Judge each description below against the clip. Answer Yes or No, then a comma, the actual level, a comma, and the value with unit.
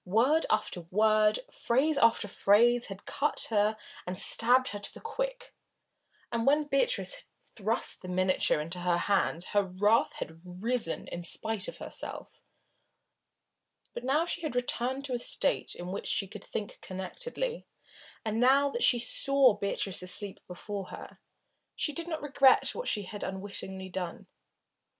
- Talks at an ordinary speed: Yes, average, 160 wpm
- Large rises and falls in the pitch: Yes, wide, 6.1 semitones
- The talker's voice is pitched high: Yes, high, 215 Hz